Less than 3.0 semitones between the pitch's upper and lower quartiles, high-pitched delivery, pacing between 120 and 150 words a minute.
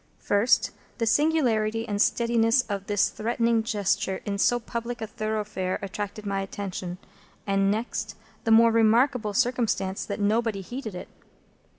Yes: narrow, 2.5 semitones; high, 220 Hz; slow, 135 wpm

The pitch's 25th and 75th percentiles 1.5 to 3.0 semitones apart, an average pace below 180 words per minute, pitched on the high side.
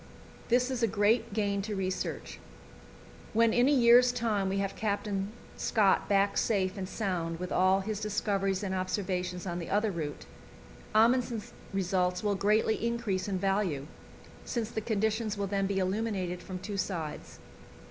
Yes: average, 2.7 semitones; average, 160 wpm; high, 200 Hz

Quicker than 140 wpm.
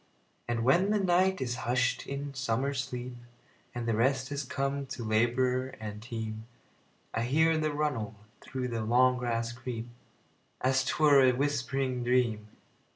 No: slow, 135 wpm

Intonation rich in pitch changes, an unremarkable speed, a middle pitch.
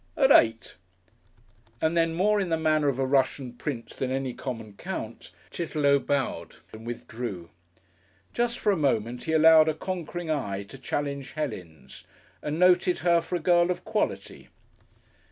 Yes: wide, 5.7 semitones; average, 160 wpm; medium, 145 Hz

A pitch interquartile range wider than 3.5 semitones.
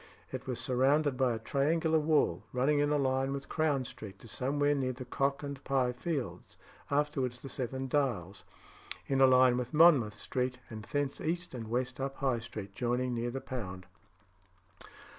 No: narrow, 2.6 semitones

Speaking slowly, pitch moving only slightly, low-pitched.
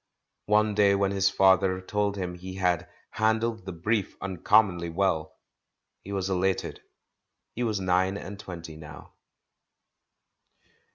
Yes: slow, 130 wpm; narrow, 2.2 semitones; very low, 95 Hz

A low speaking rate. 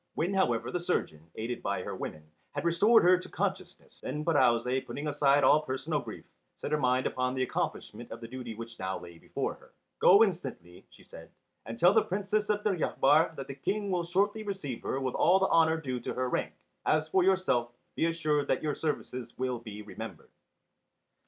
No: average, 195 wpm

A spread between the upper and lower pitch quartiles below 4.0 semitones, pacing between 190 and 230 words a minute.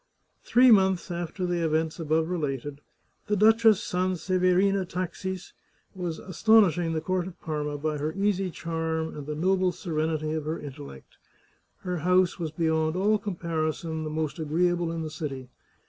No: average, 2.9 semitones; average, 150 wpm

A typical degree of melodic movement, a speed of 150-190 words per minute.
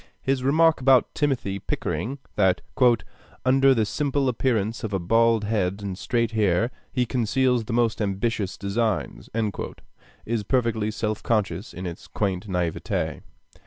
No: average, 4.2 semitones; slow, 135 wpm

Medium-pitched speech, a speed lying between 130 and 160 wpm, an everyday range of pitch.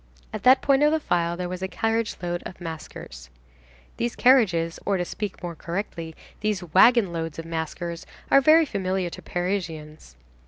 No: medium, 180 Hz; average, 170 wpm; average, 4.7 semitones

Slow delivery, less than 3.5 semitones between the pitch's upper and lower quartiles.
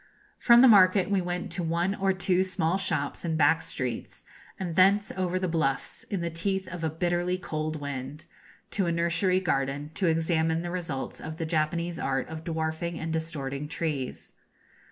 No: average, 175 wpm; average, 2.7 semitones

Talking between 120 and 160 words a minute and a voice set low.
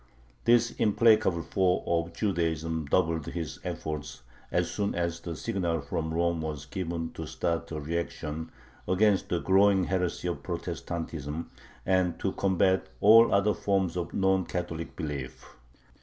Yes: average, 140 wpm; very low, 85 Hz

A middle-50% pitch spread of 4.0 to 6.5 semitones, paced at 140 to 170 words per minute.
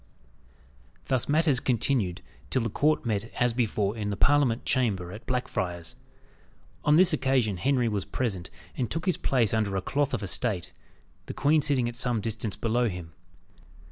Yes: average, 4.6 semitones; average, 165 wpm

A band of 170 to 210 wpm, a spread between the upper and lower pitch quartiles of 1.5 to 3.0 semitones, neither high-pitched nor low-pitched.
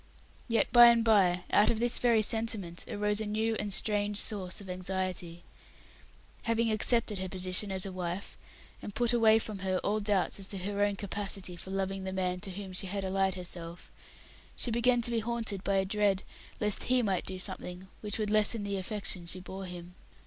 No: average, 195 wpm; narrow, 2.6 semitones; high, 200 Hz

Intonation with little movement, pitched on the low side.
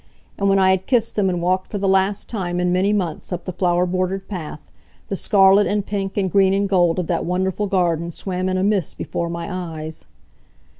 No: narrow, 1.8 semitones; medium, 185 Hz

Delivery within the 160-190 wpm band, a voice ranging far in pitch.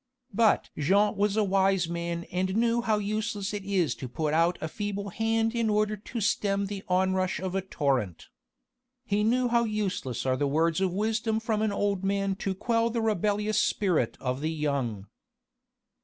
No: average, 180 wpm; average, 3.9 semitones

